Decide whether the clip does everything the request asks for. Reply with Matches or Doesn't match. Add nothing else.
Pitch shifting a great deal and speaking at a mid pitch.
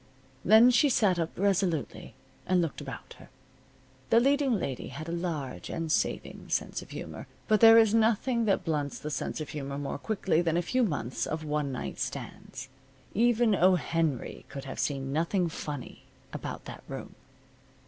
Matches